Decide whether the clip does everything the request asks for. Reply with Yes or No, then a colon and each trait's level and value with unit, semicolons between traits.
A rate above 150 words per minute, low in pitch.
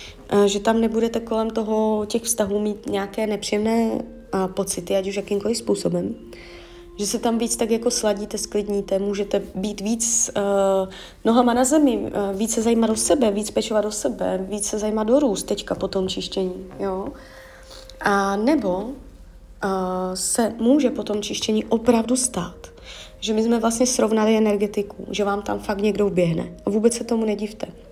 No: average, 165 wpm; high, 215 Hz